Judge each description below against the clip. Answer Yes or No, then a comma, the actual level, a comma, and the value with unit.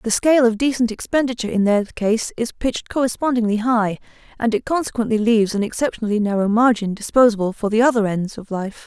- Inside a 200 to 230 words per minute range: No, average, 185 wpm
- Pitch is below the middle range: No, high, 225 Hz